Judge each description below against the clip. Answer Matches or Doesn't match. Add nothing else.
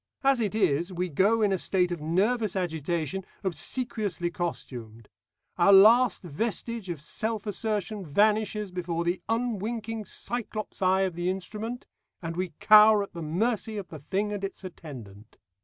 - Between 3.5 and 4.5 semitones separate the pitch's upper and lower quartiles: Matches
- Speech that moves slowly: Doesn't match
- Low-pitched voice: Doesn't match